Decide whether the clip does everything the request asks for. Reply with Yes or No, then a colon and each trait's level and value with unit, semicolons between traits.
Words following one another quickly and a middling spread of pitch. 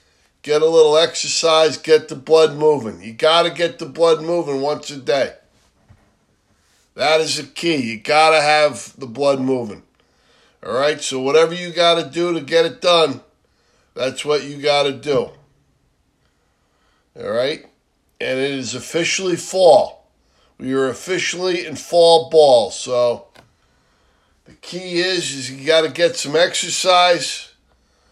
No: slow, 135 wpm; average, 4.1 semitones